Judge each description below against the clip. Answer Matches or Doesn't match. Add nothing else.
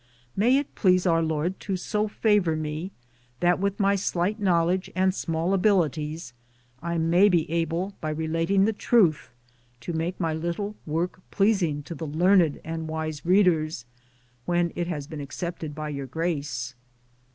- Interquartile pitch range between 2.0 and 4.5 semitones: Matches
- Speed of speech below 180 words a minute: Matches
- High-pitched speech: Doesn't match